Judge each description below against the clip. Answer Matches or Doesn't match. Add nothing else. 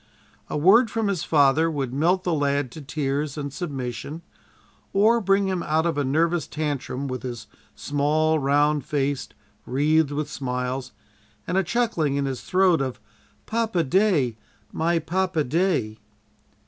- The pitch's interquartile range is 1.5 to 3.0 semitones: Doesn't match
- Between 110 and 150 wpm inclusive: Matches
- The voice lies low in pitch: Doesn't match